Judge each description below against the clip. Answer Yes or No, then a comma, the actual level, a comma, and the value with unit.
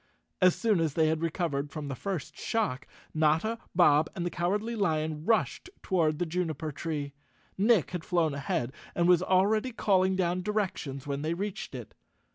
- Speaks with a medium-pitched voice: Yes, medium, 170 Hz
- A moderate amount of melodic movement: Yes, average, 3.8 semitones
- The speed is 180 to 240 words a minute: No, average, 170 wpm